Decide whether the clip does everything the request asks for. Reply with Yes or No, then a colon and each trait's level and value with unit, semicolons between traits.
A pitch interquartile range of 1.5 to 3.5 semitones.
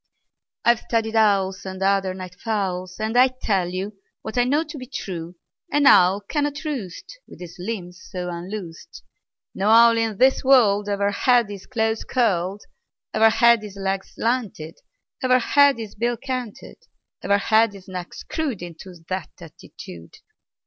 No: average, 4.2 semitones